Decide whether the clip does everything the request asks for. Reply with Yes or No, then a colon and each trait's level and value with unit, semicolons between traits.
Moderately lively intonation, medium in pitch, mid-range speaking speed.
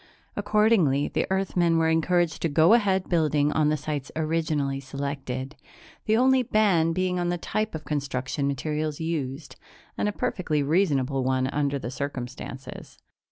Yes: average, 4.2 semitones; medium, 155 Hz; average, 150 wpm